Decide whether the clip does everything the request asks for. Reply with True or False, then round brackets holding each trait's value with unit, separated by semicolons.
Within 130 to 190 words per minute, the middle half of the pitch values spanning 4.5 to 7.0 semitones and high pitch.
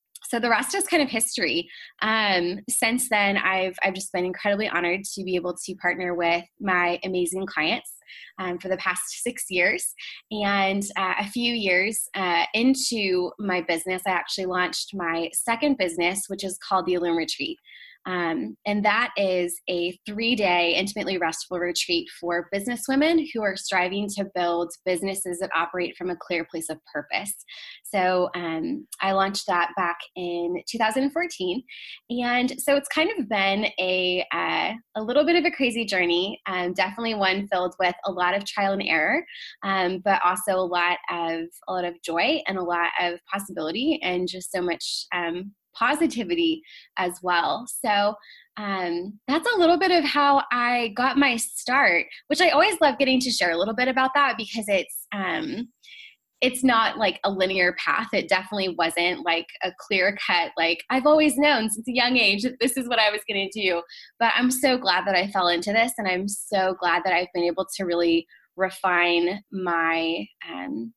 True (180 wpm; 5.3 semitones; 195 Hz)